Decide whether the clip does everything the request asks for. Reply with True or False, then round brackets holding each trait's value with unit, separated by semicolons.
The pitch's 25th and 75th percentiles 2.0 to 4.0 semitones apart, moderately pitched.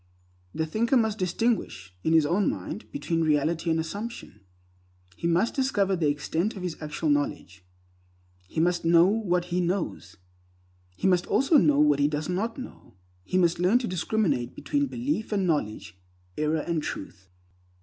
False (5.5 semitones; 175 Hz)